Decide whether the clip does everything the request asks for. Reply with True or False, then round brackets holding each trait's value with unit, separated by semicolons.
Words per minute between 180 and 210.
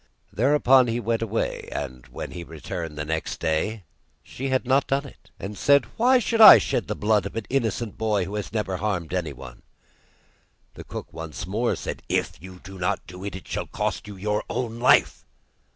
True (190 wpm)